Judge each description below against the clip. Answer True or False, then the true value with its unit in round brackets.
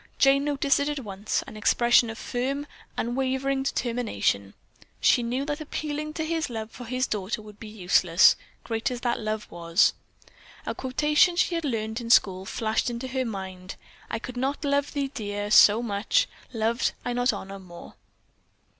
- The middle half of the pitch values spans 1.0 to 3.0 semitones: False (4.5 semitones)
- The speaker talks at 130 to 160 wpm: False (170 wpm)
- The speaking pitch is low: False (240 Hz)